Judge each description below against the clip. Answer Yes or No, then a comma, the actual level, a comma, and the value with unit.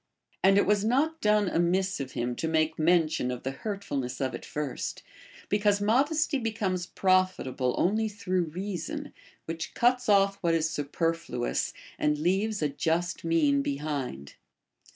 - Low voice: No, medium, 175 Hz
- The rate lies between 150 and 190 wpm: Yes, average, 155 wpm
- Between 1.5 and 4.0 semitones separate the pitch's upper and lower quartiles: No, wide, 5.6 semitones